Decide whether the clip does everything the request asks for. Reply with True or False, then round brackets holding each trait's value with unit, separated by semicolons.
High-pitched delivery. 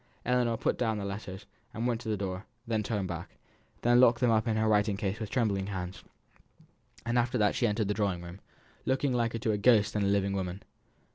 False (105 Hz)